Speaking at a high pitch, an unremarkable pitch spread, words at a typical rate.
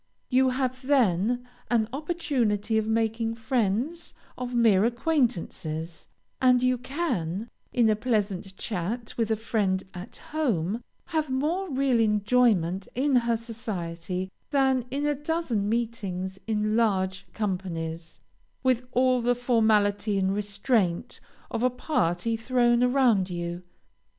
No: high, 225 Hz; average, 4.5 semitones; slow, 125 wpm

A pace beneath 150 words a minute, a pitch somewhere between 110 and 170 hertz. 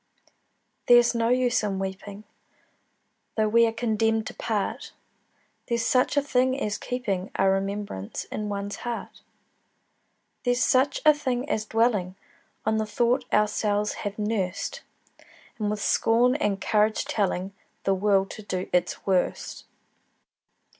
No: slow, 135 wpm; high, 215 Hz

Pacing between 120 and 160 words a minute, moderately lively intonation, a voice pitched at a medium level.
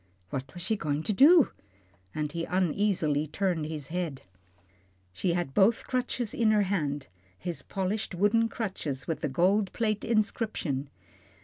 No: average, 150 wpm; wide, 5.8 semitones; medium, 180 Hz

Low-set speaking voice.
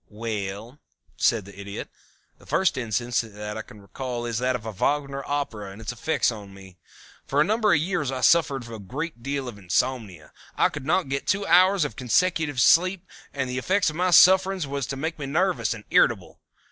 Yes: low, 130 Hz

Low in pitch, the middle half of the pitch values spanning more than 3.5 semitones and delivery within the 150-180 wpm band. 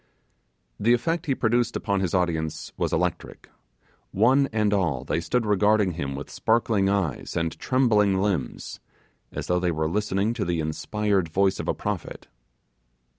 Yes: low, 100 Hz; average, 4.3 semitones; average, 155 wpm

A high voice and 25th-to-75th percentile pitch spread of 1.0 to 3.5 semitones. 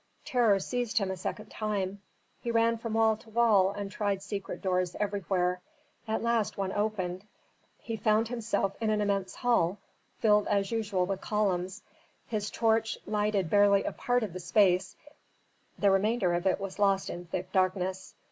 Yes: high, 205 Hz; narrow, 2.6 semitones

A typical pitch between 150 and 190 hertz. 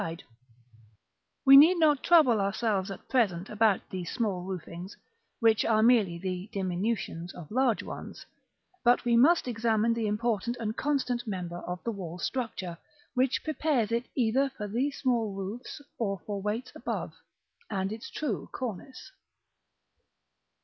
No: high, 220 Hz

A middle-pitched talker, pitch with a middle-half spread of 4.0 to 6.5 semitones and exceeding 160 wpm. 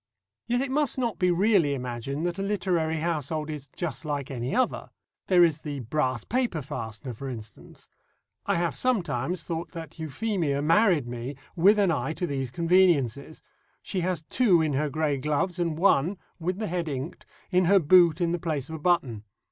Yes: medium, 160 Hz; average, 4.5 semitones; average, 185 wpm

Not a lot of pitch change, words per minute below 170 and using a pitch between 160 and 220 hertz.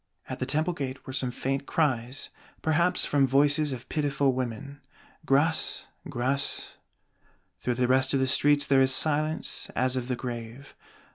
No: narrow, 2.2 semitones; average, 155 wpm; low, 135 Hz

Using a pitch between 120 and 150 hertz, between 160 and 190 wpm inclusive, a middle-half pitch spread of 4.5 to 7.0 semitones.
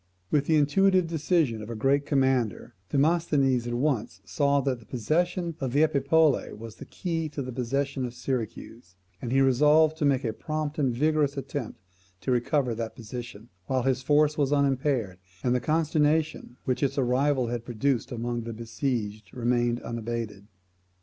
No: low, 135 Hz; average, 165 wpm; average, 3.8 semitones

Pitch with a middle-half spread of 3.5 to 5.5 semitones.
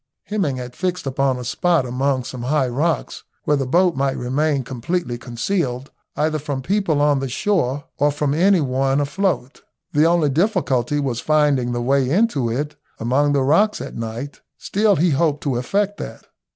Yes: average, 4.5 semitones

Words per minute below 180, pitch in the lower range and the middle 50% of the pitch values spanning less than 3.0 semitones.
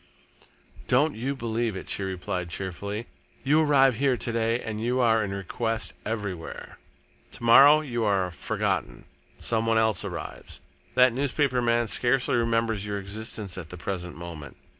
No: average, 155 wpm; low, 115 Hz; average, 3.9 semitones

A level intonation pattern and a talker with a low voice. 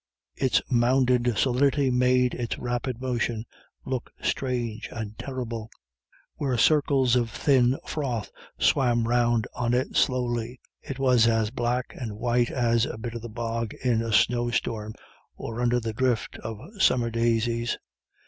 Yes: narrow, 1.7 semitones; low, 120 Hz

